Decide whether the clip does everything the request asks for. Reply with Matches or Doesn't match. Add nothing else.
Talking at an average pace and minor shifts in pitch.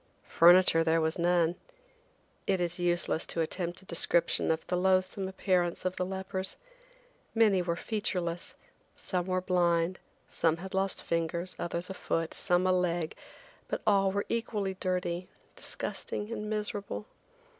Matches